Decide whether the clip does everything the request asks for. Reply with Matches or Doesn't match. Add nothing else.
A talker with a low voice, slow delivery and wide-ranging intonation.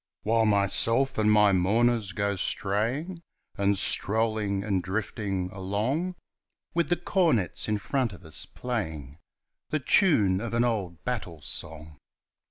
Doesn't match